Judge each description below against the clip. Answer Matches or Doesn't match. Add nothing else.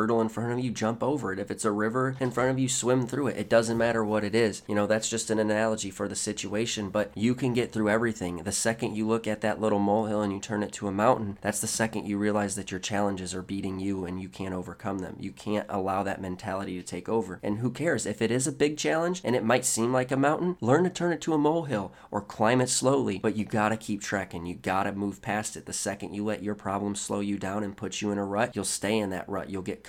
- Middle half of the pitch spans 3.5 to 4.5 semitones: Doesn't match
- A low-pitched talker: Matches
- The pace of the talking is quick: Matches